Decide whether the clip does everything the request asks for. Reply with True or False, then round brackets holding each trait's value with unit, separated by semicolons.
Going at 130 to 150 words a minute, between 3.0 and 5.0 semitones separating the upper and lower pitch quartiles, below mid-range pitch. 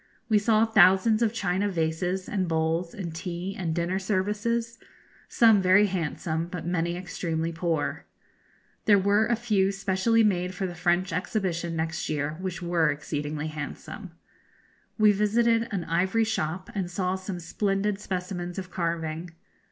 False (145 wpm; 3.4 semitones; 185 Hz)